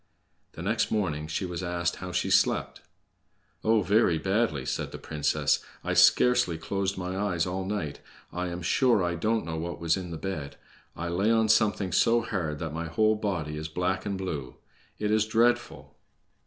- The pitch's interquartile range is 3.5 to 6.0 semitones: Yes, average, 4.3 semitones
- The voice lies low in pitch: Yes, very low, 90 Hz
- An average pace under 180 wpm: No, average, 185 wpm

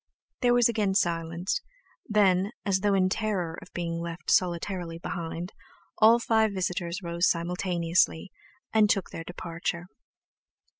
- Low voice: No, medium, 180 Hz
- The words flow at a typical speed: No, slow, 130 wpm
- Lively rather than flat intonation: No, average, 3.2 semitones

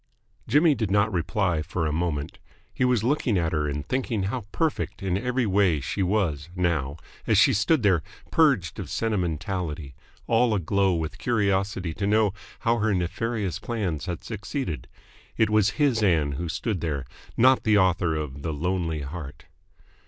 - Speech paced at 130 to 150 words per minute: No, average, 165 wpm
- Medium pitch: No, very low, 95 Hz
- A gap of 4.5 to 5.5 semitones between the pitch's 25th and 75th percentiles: Yes, average, 5.2 semitones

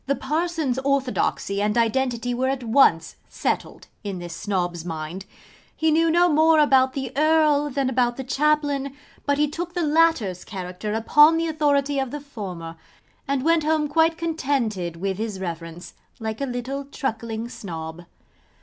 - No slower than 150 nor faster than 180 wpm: Yes, average, 160 wpm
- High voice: Yes, very high, 265 Hz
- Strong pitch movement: Yes, wide, 6.6 semitones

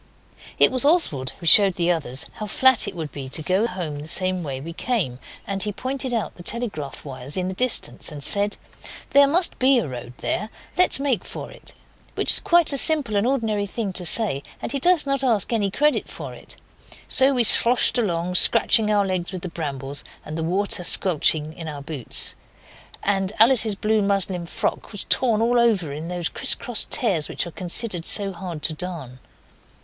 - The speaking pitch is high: Yes, high, 195 Hz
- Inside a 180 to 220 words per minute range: Yes, average, 200 wpm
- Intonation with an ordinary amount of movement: No, wide, 6.3 semitones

